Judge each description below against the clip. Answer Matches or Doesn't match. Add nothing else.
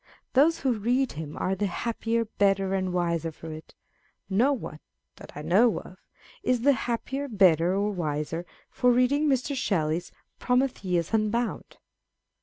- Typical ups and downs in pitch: Doesn't match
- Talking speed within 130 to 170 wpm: Matches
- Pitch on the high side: Matches